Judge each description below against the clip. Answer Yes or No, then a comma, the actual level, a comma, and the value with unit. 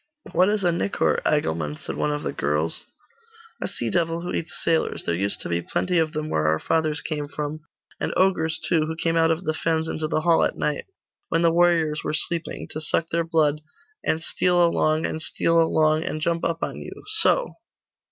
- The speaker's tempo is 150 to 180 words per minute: No, fast, 205 wpm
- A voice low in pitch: No, medium, 160 Hz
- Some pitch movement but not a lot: No, narrow, 1.7 semitones